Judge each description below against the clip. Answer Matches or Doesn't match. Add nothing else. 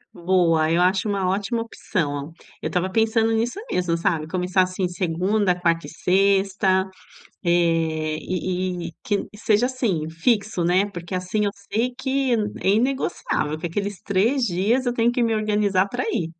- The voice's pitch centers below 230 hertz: Matches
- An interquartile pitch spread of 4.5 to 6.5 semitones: Doesn't match